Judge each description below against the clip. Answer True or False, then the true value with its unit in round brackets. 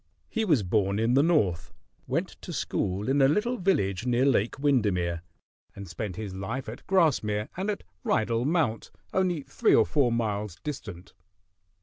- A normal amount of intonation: False (6.8 semitones)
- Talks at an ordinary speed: True (160 wpm)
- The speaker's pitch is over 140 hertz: False (115 Hz)